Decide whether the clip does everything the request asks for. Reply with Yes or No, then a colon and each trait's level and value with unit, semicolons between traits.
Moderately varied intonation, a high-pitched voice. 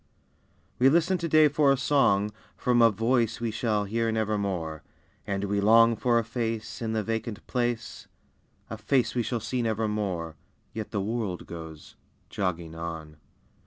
No: average, 3.1 semitones; low, 110 Hz